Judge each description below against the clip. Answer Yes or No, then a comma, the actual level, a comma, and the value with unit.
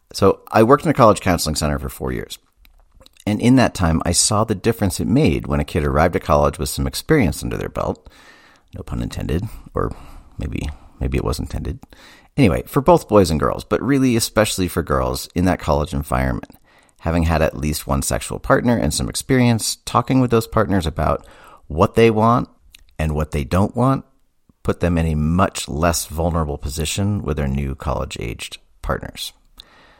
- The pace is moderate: Yes, average, 185 wpm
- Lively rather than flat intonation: Yes, wide, 6.2 semitones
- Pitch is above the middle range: No, very low, 80 Hz